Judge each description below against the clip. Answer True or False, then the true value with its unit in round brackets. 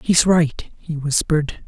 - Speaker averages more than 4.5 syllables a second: False (4.0 syllables/s)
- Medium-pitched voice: True (155 Hz)